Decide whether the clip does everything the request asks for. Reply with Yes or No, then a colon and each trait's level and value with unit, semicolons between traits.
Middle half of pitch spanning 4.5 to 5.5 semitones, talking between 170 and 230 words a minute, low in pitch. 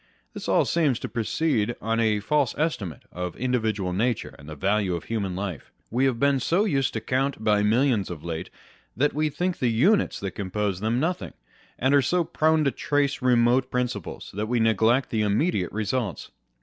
Yes: average, 5.1 semitones; average, 190 wpm; low, 115 Hz